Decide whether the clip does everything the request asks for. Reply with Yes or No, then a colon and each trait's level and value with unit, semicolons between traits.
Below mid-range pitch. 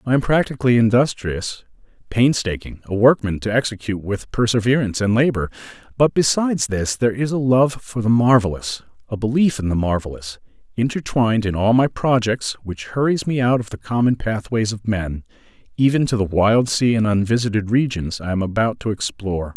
Yes: low, 115 Hz